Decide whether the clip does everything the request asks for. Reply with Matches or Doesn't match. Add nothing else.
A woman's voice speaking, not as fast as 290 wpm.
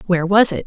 Matches